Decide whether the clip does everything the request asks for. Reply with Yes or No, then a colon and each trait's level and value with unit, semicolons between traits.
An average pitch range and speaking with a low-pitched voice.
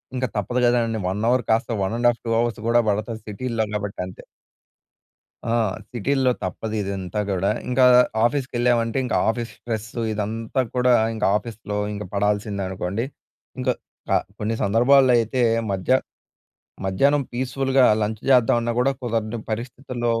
Yes: average, 3.0 semitones; low, 115 Hz